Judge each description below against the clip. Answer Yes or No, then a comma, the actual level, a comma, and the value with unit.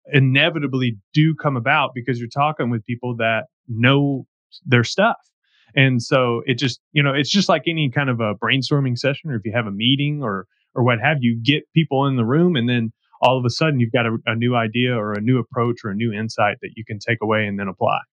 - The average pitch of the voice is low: Yes, low, 125 Hz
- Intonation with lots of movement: No, average, 3.3 semitones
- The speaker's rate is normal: No, fast, 240 wpm